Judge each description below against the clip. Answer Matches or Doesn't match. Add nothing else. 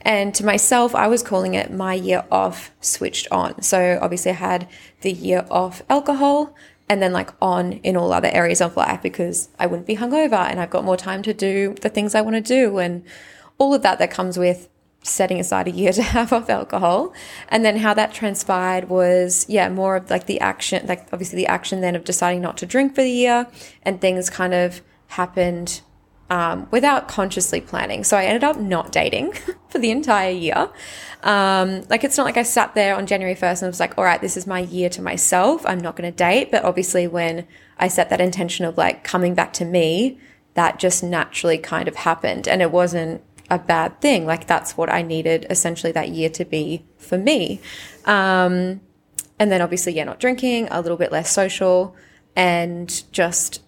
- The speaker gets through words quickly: Matches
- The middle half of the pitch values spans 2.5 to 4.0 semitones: Matches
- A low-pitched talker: Doesn't match